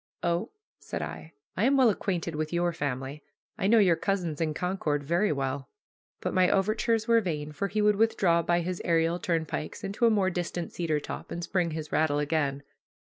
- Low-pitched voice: No, medium, 170 Hz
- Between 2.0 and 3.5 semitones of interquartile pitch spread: No, average, 4.2 semitones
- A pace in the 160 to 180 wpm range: No, average, 190 wpm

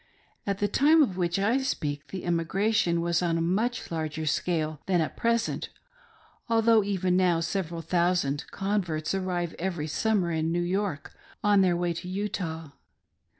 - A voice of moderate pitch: Yes, medium, 180 Hz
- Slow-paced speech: No, average, 160 wpm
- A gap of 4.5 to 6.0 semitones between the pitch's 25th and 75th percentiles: No, average, 3.3 semitones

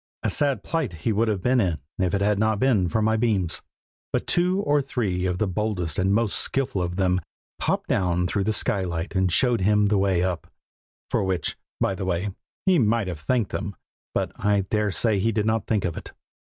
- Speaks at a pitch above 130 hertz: No, low, 100 Hz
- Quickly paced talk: Yes, fast, 215 wpm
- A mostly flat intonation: No, average, 3.5 semitones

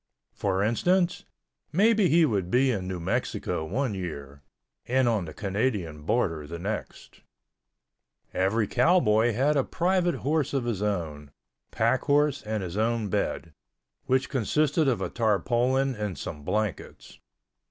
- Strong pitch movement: Yes, wide, 6.3 semitones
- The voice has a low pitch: Yes, low, 110 Hz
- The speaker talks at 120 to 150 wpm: Yes, average, 140 wpm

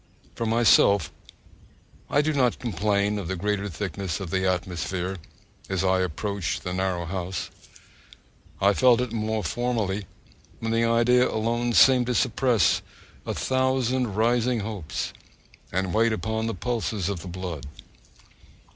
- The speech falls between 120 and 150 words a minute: Yes, average, 140 wpm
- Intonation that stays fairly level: No, average, 3.9 semitones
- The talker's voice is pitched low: Yes, low, 105 Hz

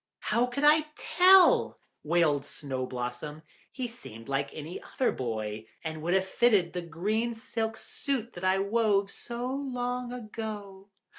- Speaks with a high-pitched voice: Yes, high, 200 Hz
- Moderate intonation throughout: No, wide, 7.5 semitones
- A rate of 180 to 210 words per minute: No, average, 150 wpm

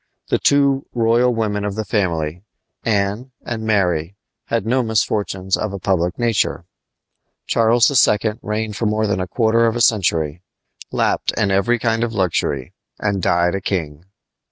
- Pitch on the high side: No, low, 105 Hz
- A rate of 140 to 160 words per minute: Yes, average, 155 wpm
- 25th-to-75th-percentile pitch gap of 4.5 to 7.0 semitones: No, average, 3.5 semitones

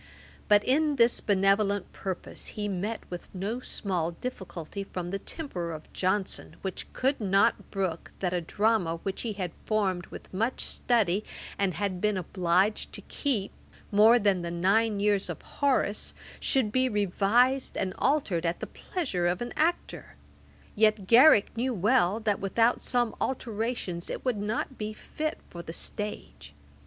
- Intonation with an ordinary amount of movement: Yes, average, 4.0 semitones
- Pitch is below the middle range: No, high, 205 Hz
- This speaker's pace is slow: No, average, 155 wpm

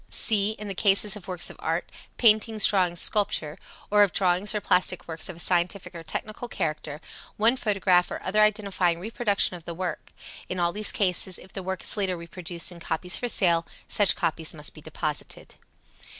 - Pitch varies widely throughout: No, average, 3.3 semitones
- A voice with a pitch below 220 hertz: Yes, medium, 185 Hz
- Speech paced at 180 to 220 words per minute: Yes, average, 190 wpm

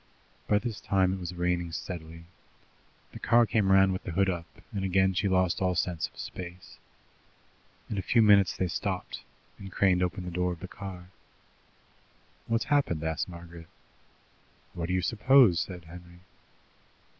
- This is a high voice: No, very low, 90 Hz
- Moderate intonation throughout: No, narrow, 2.0 semitones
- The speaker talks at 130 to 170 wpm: Yes, average, 165 wpm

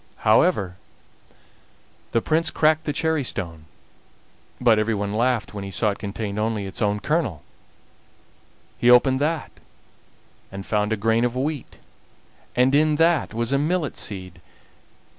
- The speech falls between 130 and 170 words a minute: Yes, average, 140 wpm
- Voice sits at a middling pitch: No, low, 115 Hz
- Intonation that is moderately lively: No, wide, 6.2 semitones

